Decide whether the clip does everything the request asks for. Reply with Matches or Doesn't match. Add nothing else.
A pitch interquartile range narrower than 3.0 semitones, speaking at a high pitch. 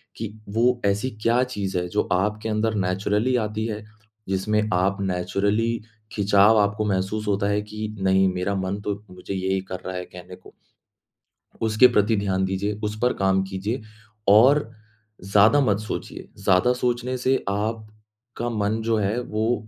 Doesn't match